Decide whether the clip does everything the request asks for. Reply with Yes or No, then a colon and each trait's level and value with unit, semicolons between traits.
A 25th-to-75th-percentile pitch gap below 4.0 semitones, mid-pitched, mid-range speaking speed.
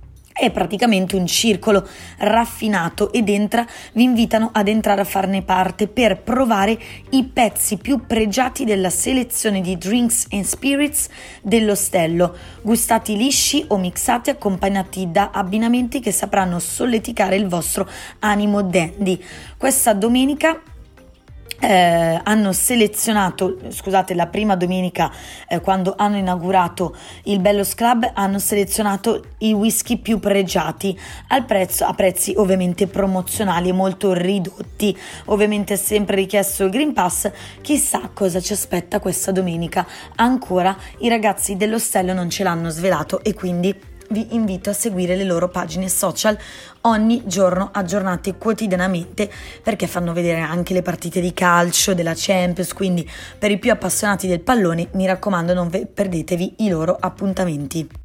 No: average, 2.9 semitones; high, 200 Hz; average, 135 wpm